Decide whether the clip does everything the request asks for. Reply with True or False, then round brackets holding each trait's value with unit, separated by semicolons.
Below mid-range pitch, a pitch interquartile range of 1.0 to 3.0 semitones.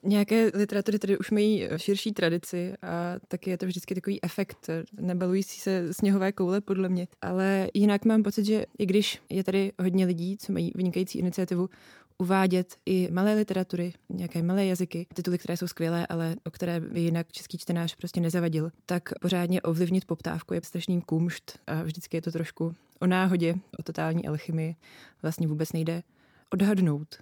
False (180 Hz; 2.4 semitones)